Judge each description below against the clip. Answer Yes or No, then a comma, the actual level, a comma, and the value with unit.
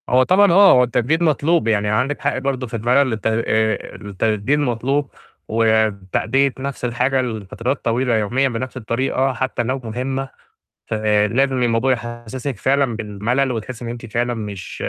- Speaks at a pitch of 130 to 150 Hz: No, low, 120 Hz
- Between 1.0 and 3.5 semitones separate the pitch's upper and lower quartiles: Yes, average, 3.2 semitones